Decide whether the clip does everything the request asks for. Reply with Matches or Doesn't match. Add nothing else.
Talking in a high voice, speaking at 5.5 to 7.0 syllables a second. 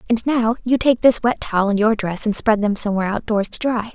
Matches